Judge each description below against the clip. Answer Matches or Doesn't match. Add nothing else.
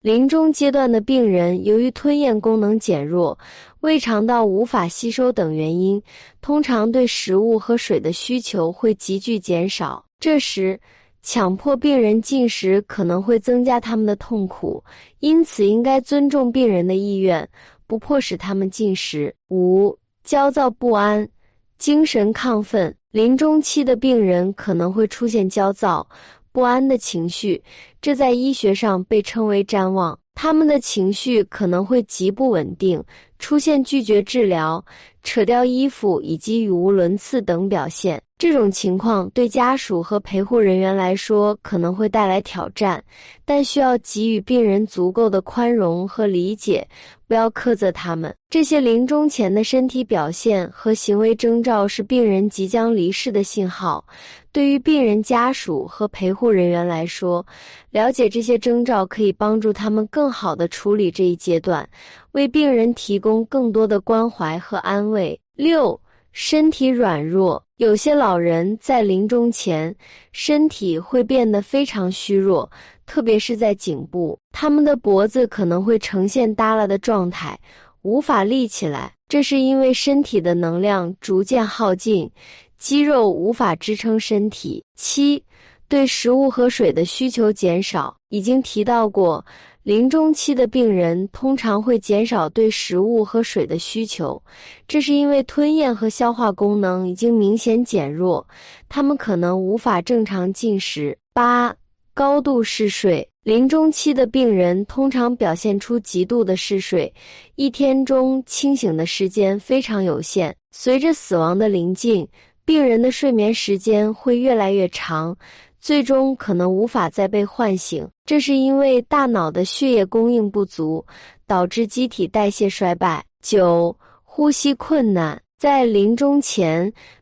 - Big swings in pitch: Doesn't match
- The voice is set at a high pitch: Matches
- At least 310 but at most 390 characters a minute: Doesn't match